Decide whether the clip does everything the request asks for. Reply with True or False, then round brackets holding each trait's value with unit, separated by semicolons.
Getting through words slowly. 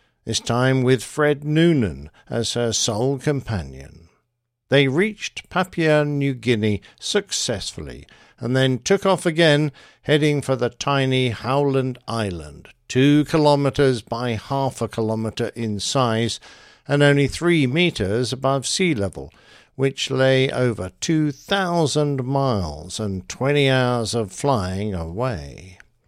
True (120 wpm)